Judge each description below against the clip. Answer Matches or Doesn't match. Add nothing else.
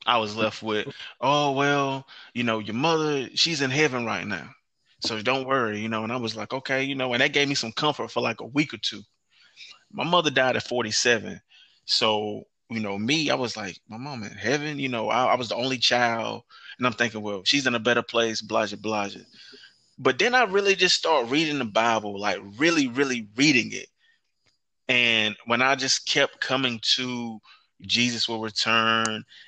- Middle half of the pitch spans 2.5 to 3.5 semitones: Doesn't match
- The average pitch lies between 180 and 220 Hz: Doesn't match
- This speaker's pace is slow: Doesn't match